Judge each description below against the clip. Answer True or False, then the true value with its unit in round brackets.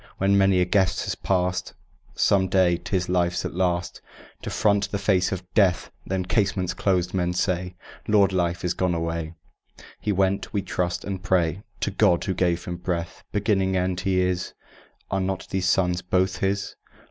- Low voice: True (95 Hz)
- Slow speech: False (175 wpm)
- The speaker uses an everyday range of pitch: False (1.5 semitones)